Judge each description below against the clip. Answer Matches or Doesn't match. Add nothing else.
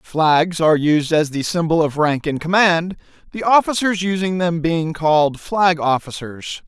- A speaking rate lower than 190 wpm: Matches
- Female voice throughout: Doesn't match